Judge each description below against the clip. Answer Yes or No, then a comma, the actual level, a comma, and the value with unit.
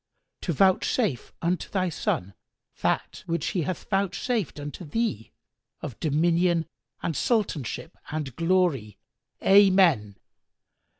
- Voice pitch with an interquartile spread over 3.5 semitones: Yes, average, 4.6 semitones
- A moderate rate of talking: No, slow, 105 wpm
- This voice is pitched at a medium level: Yes, medium, 170 Hz